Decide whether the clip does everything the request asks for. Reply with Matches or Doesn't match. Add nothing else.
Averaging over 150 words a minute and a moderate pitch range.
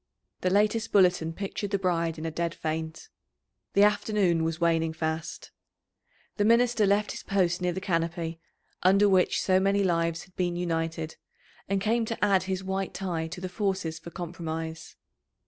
Matches